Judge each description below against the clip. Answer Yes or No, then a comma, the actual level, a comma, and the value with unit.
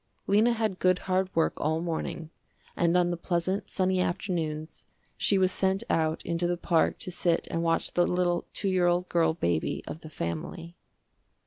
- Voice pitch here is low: No, medium, 175 Hz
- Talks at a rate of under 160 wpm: No, average, 180 wpm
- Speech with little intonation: Yes, narrow, 2.0 semitones